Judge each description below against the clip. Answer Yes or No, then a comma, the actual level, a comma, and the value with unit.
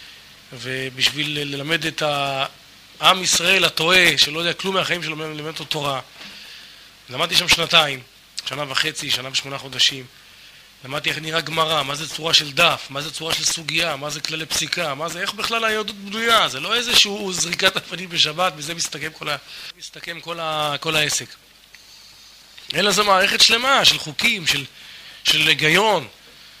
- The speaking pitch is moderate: Yes, medium, 160 Hz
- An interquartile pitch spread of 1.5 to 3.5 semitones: Yes, average, 3.2 semitones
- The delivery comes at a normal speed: No, fast, 160 wpm